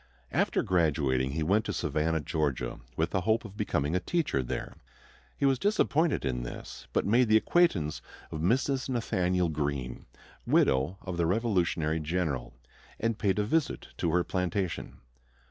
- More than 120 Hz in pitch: No, very low, 90 Hz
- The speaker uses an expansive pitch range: Yes, wide, 6.3 semitones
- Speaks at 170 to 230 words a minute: No, average, 155 wpm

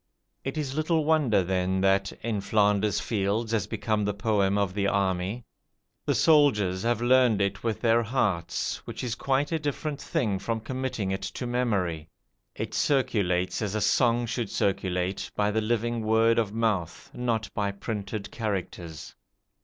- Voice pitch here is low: Yes, low, 110 Hz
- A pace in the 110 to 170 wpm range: Yes, average, 160 wpm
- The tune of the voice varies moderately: Yes, average, 3.6 semitones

